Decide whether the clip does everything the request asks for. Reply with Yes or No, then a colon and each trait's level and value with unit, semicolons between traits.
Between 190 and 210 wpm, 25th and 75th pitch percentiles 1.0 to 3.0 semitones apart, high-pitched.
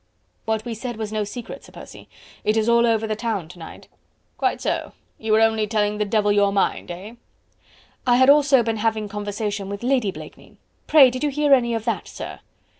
Yes: fast, 205 wpm; narrow, 2.4 semitones; high, 220 Hz